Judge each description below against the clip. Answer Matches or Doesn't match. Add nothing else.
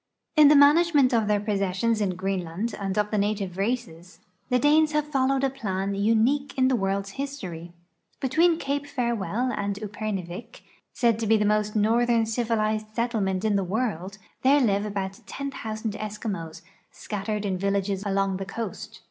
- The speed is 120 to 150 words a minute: Doesn't match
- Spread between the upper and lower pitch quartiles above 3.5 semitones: Matches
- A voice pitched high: Matches